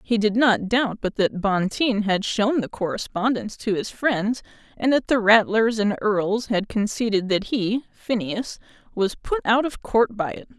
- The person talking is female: Yes, female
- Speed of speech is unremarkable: Yes, average, 180 wpm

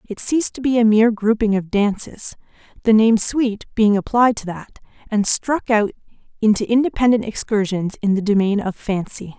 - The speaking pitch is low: No, high, 215 Hz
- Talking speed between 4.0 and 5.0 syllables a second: No, 5.3 syllables/s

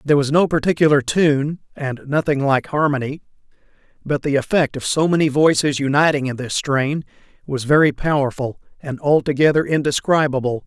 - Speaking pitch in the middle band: Yes, medium, 145 Hz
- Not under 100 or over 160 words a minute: Yes, average, 145 wpm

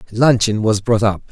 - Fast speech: No, average, 180 wpm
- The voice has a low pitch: Yes, low, 110 Hz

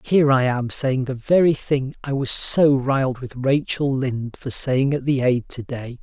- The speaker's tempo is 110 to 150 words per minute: No, average, 200 wpm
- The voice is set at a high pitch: No, low, 135 Hz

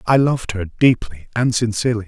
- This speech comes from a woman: No, male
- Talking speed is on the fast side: No, average, 175 wpm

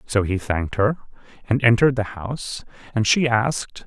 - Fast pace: No, average, 170 wpm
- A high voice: No, low, 115 Hz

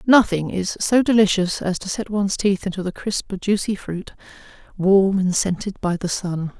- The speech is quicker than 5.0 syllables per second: No, 4.8 syllables/s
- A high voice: Yes, high, 195 Hz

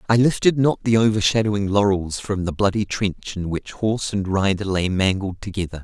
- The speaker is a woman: No, male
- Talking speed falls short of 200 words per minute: Yes, average, 185 wpm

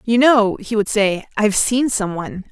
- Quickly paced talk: No, average, 190 wpm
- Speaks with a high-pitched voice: Yes, high, 215 Hz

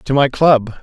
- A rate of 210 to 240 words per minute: Yes, fast, 220 wpm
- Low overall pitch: Yes, low, 130 Hz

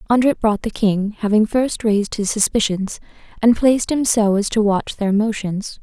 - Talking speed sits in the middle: Yes, average, 185 wpm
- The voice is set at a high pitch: Yes, high, 215 Hz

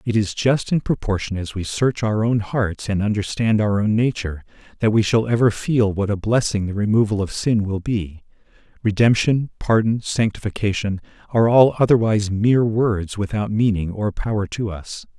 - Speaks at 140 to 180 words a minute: Yes, average, 175 wpm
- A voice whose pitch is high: No, low, 105 Hz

